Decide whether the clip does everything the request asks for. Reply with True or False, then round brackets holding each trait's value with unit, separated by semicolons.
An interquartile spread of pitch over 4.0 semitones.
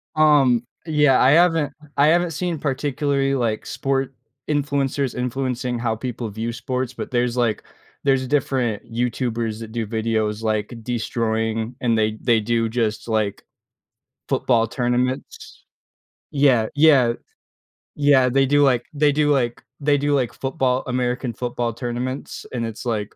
False (3.1 semitones)